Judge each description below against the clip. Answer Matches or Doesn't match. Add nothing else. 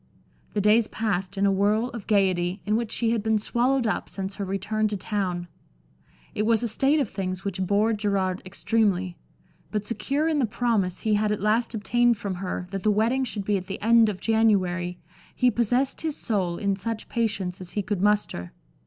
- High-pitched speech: Matches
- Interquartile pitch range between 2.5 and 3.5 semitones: Matches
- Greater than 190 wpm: Matches